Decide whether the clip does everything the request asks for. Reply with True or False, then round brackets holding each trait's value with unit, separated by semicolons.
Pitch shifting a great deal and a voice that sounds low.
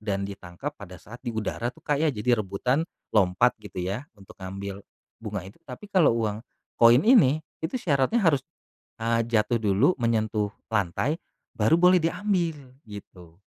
True (6.6 semitones; 115 Hz)